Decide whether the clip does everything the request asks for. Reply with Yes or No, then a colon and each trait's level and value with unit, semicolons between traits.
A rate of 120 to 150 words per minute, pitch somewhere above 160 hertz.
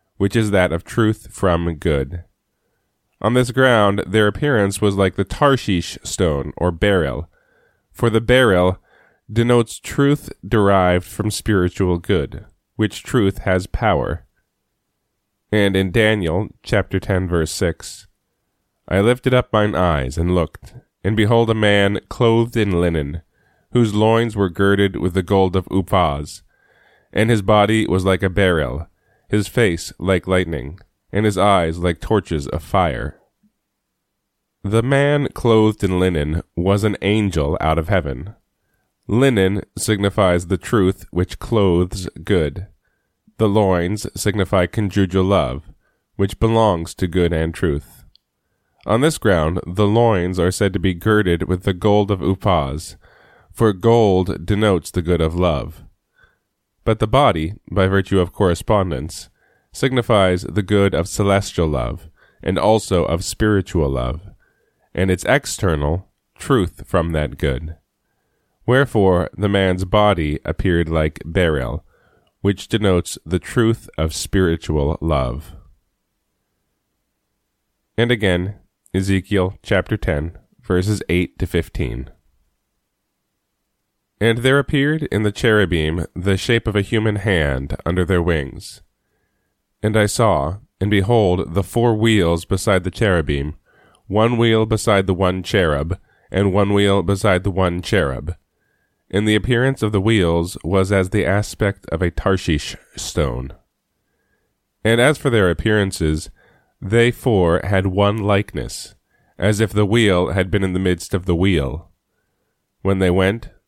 No: slow, 135 wpm; very low, 95 Hz